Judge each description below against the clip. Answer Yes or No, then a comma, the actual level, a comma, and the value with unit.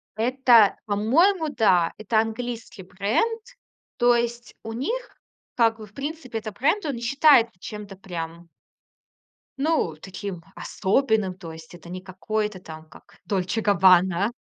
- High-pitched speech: Yes, high, 215 Hz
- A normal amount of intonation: Yes, average, 4.6 semitones